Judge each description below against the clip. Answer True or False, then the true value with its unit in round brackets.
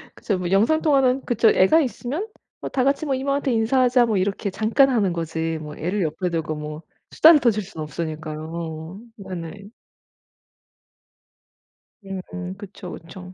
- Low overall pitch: False (195 Hz)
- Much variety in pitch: True (7.3 semitones)